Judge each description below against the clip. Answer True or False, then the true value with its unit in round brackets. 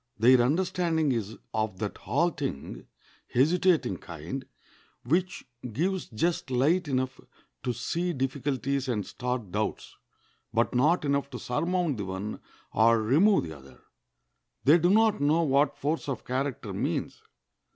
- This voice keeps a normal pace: False (130 wpm)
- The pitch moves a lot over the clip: True (6.1 semitones)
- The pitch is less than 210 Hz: True (135 Hz)